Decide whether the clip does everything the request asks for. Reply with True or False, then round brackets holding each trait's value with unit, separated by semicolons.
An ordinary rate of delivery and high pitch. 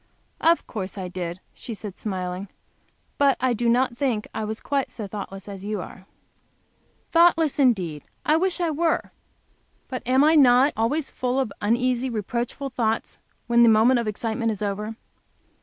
True (165 wpm; 235 Hz)